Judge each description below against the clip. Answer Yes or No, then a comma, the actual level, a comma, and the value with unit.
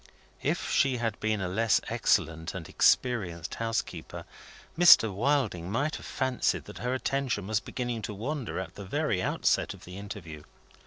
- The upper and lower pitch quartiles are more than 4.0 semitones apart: Yes, average, 5.3 semitones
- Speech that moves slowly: No, average, 160 wpm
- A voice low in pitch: Yes, low, 110 Hz